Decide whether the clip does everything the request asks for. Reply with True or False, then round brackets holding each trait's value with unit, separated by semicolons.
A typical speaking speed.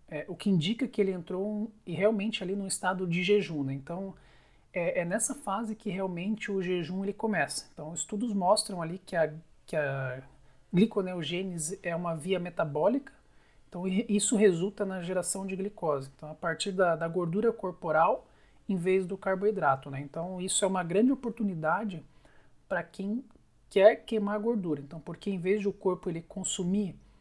True (175 wpm)